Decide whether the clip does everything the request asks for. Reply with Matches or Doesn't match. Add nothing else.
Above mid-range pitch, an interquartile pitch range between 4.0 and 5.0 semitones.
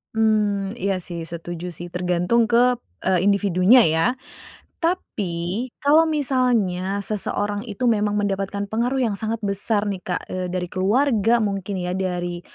Doesn't match